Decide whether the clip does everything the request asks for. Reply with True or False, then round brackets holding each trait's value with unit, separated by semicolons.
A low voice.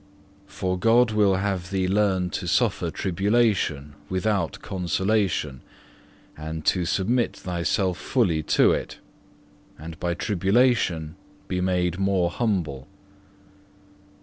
True (95 Hz)